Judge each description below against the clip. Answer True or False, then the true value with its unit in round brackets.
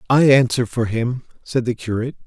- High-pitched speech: False (120 Hz)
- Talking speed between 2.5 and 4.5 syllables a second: False (5.5 syllables/s)